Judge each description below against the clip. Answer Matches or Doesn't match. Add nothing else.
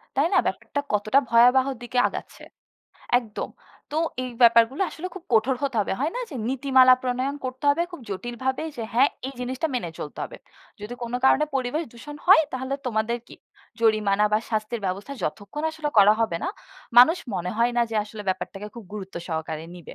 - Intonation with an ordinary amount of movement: Matches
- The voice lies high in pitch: Matches